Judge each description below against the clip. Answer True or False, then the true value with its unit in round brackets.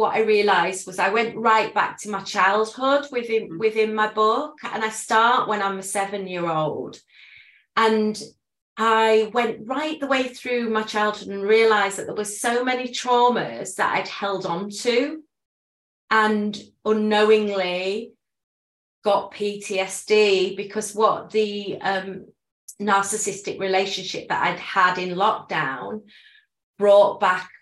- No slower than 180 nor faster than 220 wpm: False (135 wpm)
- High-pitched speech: True (215 Hz)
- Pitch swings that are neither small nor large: False (2.2 semitones)